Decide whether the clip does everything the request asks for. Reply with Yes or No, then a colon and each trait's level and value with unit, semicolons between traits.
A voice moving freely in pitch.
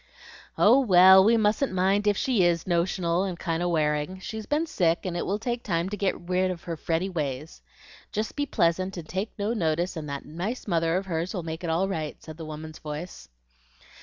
No: average, 3.4 semitones